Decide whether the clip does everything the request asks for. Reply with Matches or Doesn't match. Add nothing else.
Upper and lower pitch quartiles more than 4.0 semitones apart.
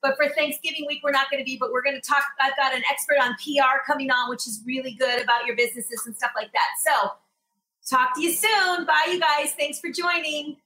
Doesn't match